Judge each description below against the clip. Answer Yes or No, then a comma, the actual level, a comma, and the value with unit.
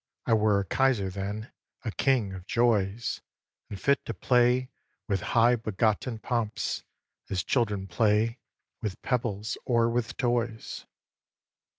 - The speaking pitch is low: Yes, low, 110 Hz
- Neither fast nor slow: No, slow, 125 wpm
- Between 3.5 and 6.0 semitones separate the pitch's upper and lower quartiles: No, average, 3.0 semitones